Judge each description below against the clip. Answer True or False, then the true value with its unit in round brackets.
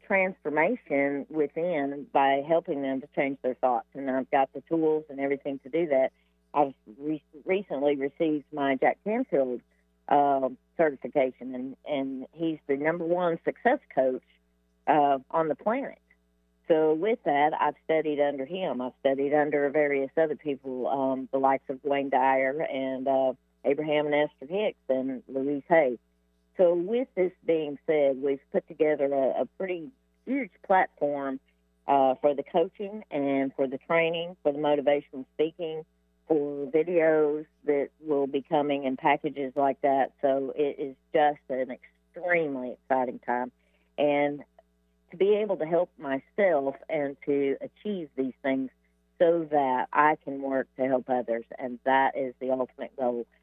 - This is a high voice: False (140 Hz)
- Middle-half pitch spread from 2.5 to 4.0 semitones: True (2.9 semitones)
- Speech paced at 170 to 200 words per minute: False (155 wpm)